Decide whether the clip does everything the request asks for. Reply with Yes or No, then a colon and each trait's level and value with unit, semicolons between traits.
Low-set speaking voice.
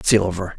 Yes: very low, 95 Hz